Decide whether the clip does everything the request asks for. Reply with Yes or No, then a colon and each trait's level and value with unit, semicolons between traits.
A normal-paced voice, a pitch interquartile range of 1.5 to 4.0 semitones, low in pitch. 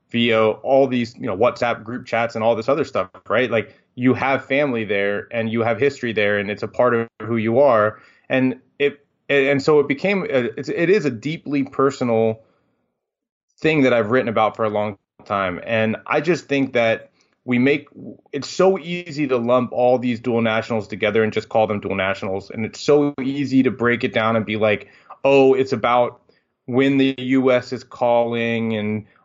Yes: average, 195 wpm; average, 3.3 semitones; low, 120 Hz